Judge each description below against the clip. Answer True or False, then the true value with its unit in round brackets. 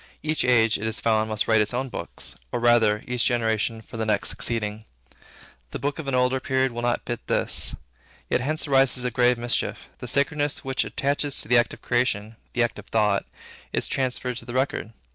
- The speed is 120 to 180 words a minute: False (205 wpm)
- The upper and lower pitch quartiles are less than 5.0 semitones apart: True (2.9 semitones)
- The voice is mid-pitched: False (120 Hz)